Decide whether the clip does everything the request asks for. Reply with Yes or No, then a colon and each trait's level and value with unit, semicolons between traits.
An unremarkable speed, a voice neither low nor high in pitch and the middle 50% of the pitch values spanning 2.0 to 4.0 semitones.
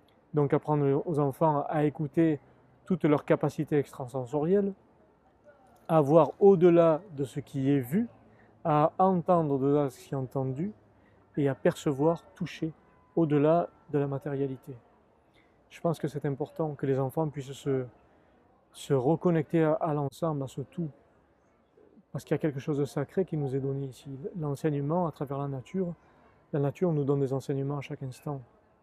Yes: average, 165 wpm; medium, 150 Hz; average, 2.9 semitones